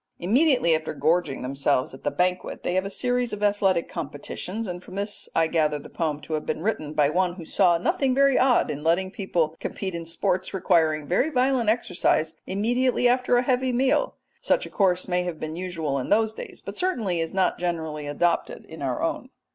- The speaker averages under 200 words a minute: No, fast, 205 wpm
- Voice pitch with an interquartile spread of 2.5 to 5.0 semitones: No, wide, 5.6 semitones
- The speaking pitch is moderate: Yes, medium, 180 Hz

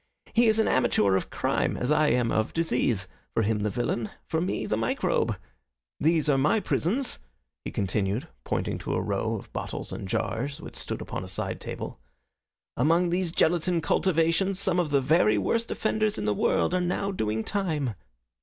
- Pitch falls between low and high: Yes, medium, 150 Hz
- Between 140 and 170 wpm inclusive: No, average, 180 wpm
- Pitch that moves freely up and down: Yes, wide, 8.3 semitones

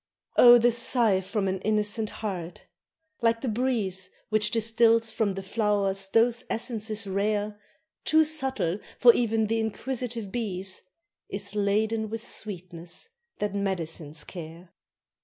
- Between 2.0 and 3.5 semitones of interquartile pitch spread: Yes, average, 2.9 semitones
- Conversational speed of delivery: No, slow, 125 wpm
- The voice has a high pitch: Yes, high, 210 Hz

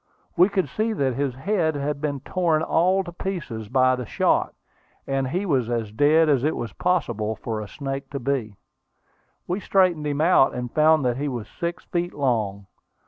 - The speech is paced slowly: No, average, 190 wpm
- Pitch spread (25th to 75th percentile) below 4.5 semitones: No, wide, 5.6 semitones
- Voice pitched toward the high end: No, medium, 140 Hz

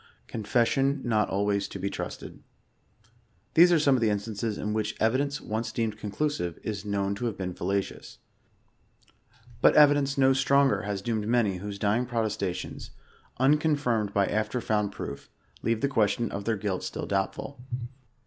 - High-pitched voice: No, low, 110 Hz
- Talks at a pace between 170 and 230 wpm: No, average, 160 wpm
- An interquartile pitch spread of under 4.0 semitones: No, average, 4.6 semitones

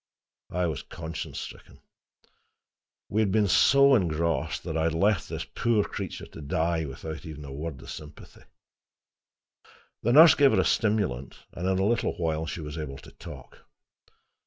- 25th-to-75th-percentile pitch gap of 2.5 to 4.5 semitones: No, average, 5.1 semitones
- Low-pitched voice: Yes, very low, 85 Hz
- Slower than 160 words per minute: No, average, 165 wpm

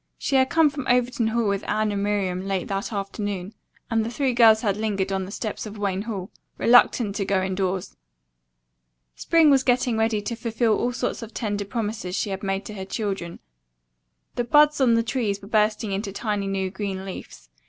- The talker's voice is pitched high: Yes, high, 210 Hz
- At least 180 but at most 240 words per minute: Yes, average, 195 wpm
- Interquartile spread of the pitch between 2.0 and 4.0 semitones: Yes, average, 3.1 semitones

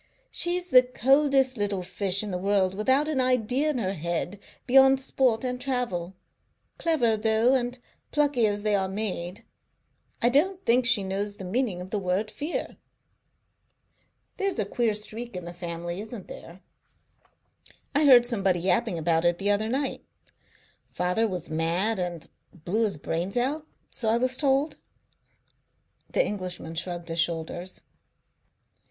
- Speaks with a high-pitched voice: Yes, high, 215 Hz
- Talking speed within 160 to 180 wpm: No, average, 150 wpm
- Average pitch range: No, wide, 6.0 semitones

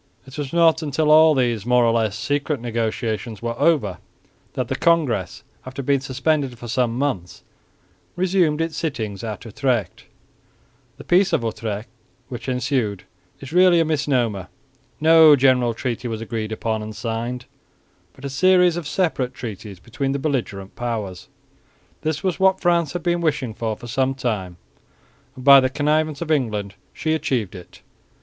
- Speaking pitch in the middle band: No, low, 130 Hz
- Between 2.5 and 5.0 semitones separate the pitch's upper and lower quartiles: No, wide, 5.5 semitones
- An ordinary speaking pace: Yes, average, 155 wpm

